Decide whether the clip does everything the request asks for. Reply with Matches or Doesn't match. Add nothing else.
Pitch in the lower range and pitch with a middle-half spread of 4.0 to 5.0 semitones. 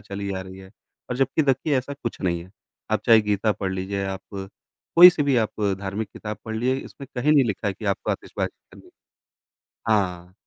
Matches